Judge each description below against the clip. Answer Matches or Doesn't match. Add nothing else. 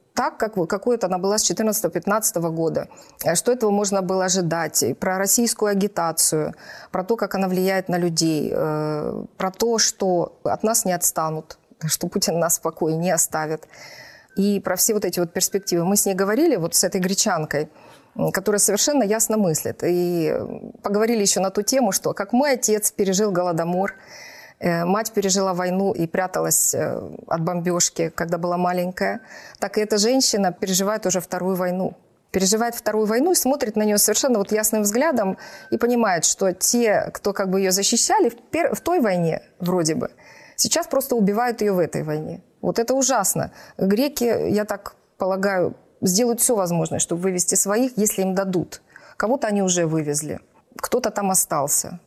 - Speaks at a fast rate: Matches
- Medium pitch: Doesn't match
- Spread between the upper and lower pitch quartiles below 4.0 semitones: Matches